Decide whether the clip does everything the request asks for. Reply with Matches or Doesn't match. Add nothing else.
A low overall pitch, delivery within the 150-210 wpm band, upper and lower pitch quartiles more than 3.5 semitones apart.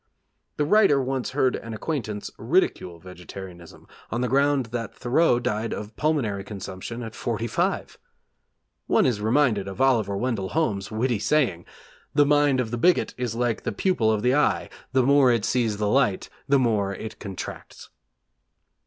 Matches